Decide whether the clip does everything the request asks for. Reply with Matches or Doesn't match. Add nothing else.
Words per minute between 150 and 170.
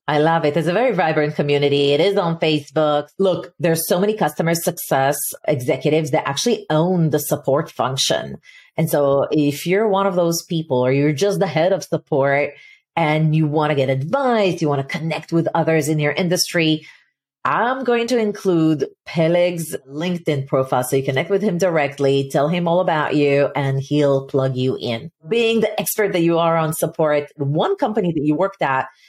Doesn't match